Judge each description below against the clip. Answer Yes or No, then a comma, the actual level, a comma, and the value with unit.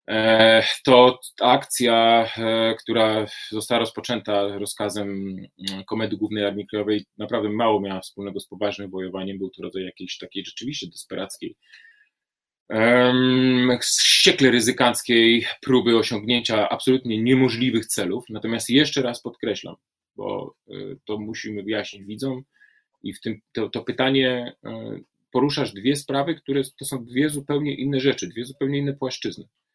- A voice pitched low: Yes, low, 115 Hz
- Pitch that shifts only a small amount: No, average, 3.6 semitones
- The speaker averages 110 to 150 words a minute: Yes, average, 125 wpm